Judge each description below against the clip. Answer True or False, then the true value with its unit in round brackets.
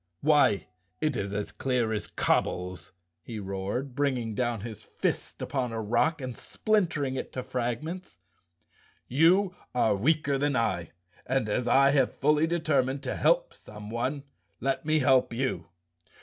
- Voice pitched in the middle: False (130 Hz)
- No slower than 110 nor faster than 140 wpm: False (150 wpm)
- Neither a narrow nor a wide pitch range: True (4.7 semitones)